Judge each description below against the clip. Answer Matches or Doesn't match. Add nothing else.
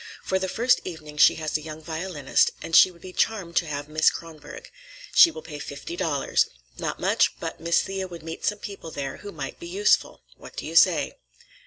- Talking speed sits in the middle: Doesn't match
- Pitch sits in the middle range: Matches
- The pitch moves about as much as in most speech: Matches